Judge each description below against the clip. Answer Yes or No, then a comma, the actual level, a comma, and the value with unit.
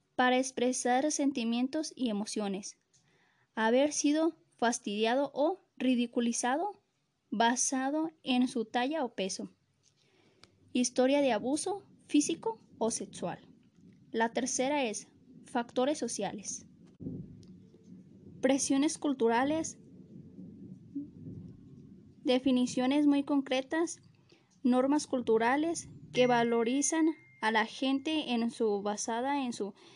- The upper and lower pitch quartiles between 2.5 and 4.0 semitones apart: Yes, average, 3.6 semitones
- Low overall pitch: No, very high, 255 Hz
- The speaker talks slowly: Yes, slow, 90 wpm